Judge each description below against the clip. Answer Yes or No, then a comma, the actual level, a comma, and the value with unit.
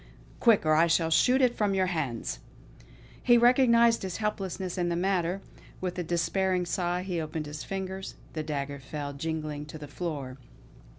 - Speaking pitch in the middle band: Yes, medium, 175 Hz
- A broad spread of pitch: No, average, 3.9 semitones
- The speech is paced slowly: No, average, 170 wpm